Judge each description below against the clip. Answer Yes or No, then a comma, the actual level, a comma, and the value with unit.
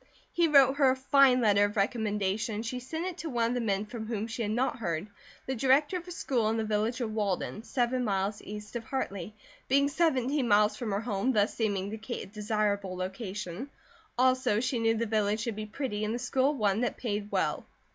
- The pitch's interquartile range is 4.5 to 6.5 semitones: No, average, 3.7 semitones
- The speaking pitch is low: No, high, 225 Hz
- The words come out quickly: Yes, fast, 220 wpm